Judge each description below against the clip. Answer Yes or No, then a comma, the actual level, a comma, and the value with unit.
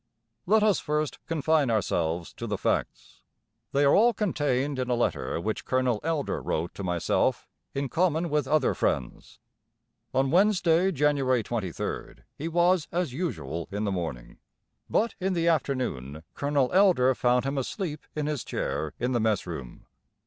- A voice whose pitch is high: No, low, 135 Hz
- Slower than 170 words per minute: Yes, average, 155 wpm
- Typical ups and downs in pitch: No, wide, 7.1 semitones